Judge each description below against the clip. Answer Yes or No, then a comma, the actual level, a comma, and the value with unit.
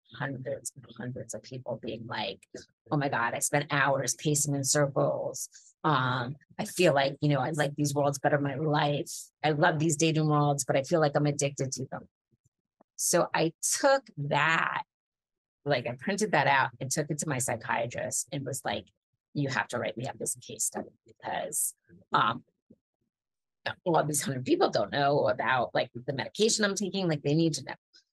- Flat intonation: Yes, narrow, 2.3 semitones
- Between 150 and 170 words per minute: No, average, 195 wpm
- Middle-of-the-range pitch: Yes, medium, 145 Hz